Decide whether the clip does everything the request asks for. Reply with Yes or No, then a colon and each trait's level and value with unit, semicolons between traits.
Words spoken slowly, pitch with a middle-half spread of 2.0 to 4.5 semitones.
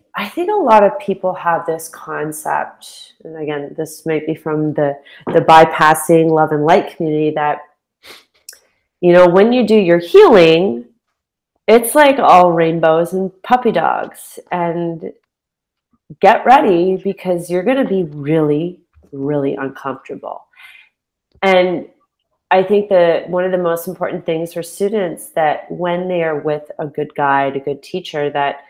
No: average, 150 wpm; average, 3.3 semitones